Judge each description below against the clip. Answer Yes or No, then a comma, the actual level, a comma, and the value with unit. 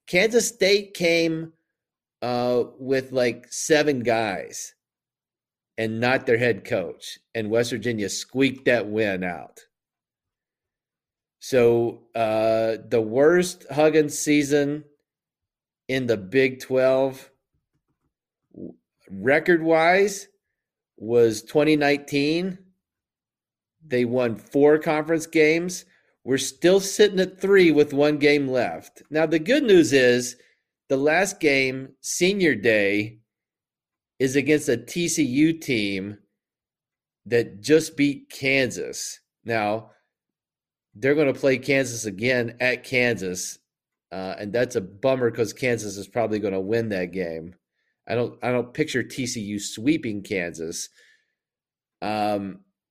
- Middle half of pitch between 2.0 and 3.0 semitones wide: No, wide, 5.5 semitones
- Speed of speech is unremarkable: No, slow, 110 wpm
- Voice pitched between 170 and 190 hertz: No, low, 130 Hz